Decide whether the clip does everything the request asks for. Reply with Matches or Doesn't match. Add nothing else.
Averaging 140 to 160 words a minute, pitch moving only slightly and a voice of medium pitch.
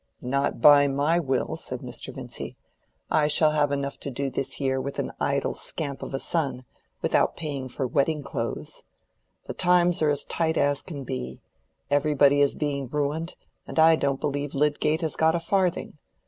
Doesn't match